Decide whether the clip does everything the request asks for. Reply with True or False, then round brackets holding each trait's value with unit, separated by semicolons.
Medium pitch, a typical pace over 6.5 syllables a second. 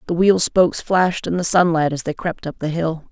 False (170 Hz; 5.6 syllables/s)